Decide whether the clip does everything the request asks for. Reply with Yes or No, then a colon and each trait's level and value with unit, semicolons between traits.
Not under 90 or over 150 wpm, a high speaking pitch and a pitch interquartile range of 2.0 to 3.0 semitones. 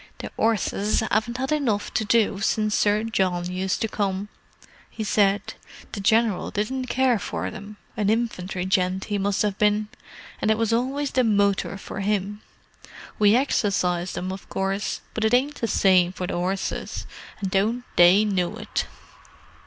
No: average, 160 wpm; high, 205 Hz; narrow, 2.6 semitones